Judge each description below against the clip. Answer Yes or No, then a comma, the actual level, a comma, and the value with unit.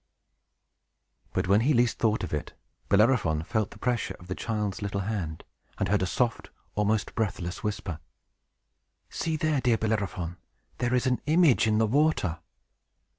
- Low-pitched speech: Yes, low, 110 Hz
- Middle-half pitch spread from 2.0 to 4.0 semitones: No, average, 4.4 semitones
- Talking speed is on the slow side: No, average, 155 wpm